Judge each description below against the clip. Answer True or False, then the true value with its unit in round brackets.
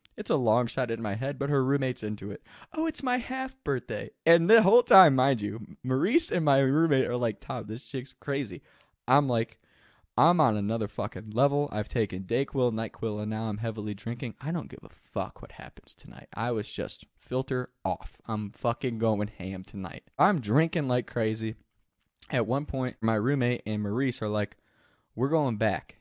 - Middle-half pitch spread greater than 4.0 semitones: True (4.6 semitones)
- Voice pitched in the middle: False (120 Hz)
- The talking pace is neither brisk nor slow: True (190 wpm)